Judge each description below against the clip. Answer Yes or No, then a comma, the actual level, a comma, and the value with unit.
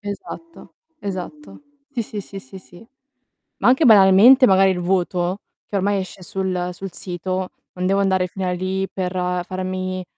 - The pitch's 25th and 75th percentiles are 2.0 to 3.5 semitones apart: No, narrow, 1.6 semitones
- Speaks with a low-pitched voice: No, high, 190 Hz